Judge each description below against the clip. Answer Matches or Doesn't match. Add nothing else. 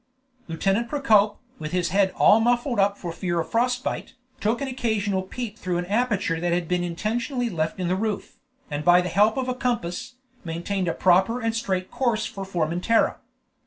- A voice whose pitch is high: Matches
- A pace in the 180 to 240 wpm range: Matches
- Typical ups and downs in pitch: Matches